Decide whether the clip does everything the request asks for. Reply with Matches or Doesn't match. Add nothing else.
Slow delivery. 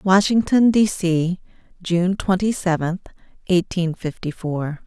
Matches